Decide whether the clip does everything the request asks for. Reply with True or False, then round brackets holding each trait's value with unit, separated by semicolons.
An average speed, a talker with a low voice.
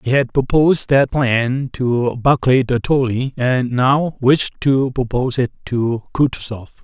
True (150 wpm; 130 Hz)